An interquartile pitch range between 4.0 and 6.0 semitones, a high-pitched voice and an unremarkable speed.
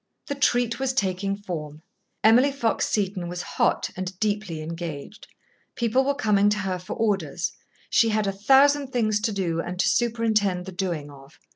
Yes: average, 4.4 semitones; high, 205 Hz; average, 170 wpm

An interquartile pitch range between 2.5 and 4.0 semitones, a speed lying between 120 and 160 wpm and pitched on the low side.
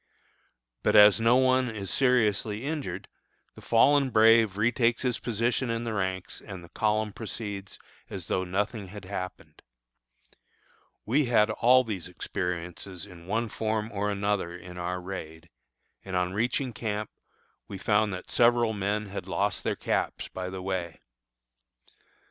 Yes: average, 3.7 semitones; average, 145 wpm; low, 105 Hz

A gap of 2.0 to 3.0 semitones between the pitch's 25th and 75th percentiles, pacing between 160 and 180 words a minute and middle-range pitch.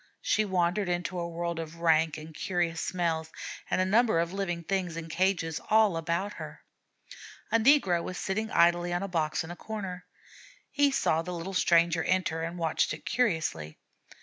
Yes: narrow, 2.6 semitones; average, 175 wpm; medium, 175 Hz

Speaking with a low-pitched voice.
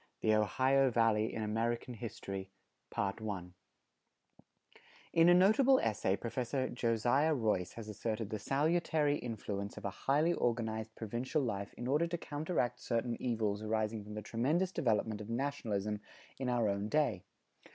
Yes: low, 115 Hz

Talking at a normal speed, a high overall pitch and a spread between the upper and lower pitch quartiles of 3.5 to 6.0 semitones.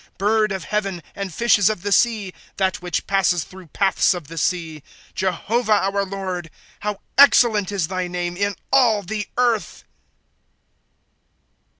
No: average, 160 wpm; high, 195 Hz; average, 2.8 semitones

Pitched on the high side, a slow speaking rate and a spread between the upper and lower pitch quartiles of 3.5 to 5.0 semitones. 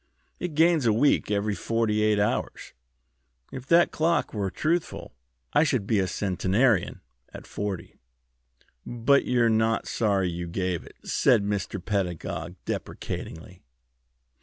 No: low, 105 Hz; slow, 130 wpm; average, 4.5 semitones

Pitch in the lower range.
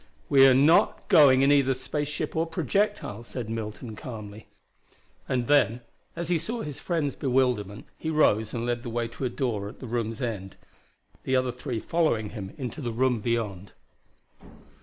Yes: low, 125 Hz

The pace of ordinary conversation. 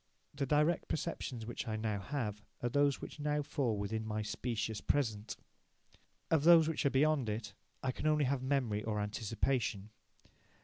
Yes: average, 165 wpm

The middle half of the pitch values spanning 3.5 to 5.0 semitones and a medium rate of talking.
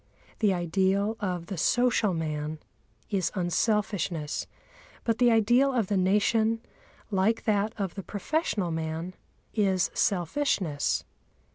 No: average, 4.0 semitones; slow, 115 wpm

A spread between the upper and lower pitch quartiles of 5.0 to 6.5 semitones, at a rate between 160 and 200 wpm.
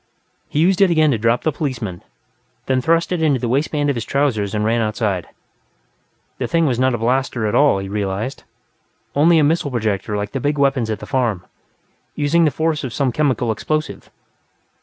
Yes: average, 5.3 semitones; average, 195 wpm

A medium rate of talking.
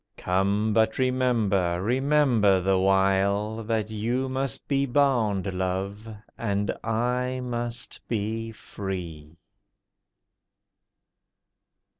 No: slow, 85 wpm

